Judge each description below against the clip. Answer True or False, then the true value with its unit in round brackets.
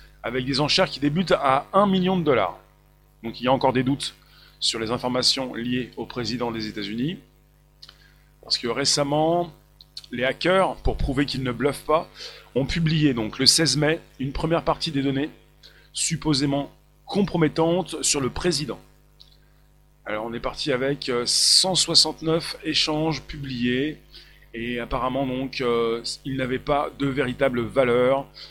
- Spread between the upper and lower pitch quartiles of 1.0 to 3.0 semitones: False (3.8 semitones)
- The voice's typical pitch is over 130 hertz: True (140 Hz)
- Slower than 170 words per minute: True (145 wpm)